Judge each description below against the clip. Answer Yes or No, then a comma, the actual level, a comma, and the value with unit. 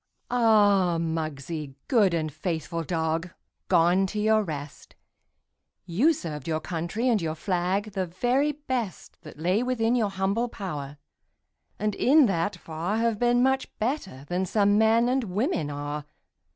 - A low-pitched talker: No, high, 190 Hz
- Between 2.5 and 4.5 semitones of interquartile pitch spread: No, wide, 5.6 semitones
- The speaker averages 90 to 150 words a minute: Yes, average, 145 wpm